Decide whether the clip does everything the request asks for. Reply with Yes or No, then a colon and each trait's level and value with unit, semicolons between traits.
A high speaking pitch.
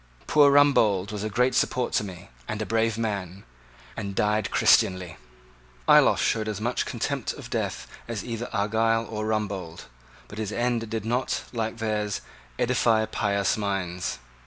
No: low, 110 Hz